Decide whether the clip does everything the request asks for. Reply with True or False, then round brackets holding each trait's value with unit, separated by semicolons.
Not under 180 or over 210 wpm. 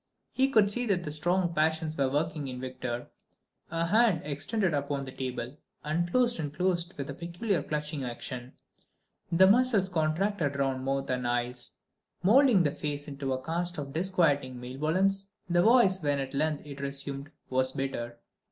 False (160 wpm)